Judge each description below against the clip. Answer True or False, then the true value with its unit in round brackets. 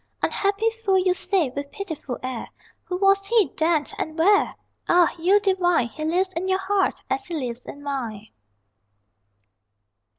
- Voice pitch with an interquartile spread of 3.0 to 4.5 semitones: False (5.4 semitones)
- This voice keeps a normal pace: True (155 wpm)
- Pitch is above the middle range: True (360 Hz)